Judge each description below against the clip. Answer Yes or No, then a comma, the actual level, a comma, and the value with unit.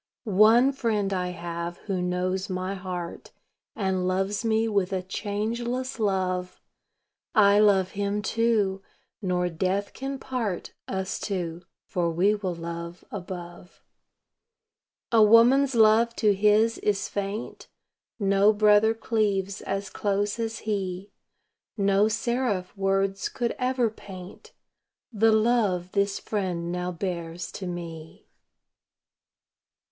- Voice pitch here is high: Yes, high, 200 Hz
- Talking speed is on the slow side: Yes, slow, 115 wpm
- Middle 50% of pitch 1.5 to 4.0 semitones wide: Yes, average, 3.0 semitones